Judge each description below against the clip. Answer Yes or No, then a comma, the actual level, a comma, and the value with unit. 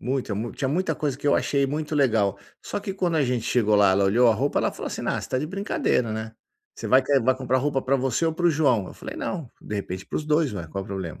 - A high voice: No, low, 130 Hz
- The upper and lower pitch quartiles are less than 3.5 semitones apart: No, wide, 5.6 semitones